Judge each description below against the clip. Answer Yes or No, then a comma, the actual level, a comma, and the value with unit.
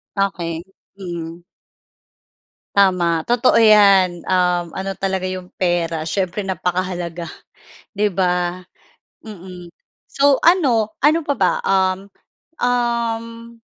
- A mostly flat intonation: No, average, 4.2 semitones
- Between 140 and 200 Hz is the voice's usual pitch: Yes, high, 190 Hz